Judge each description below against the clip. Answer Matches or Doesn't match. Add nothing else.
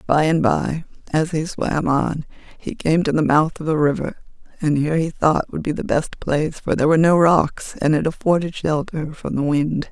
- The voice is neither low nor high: Matches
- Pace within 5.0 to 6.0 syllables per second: Matches